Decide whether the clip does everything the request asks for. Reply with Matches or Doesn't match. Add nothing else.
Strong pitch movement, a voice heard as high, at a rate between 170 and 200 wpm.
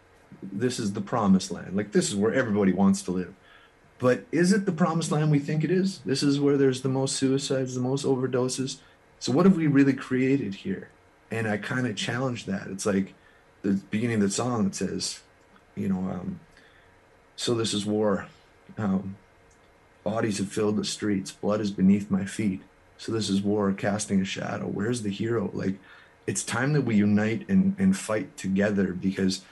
Doesn't match